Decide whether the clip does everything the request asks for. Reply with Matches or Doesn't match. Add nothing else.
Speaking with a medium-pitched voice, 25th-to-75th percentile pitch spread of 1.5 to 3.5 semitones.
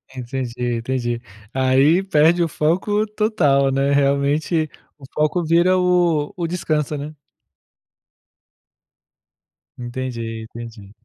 Doesn't match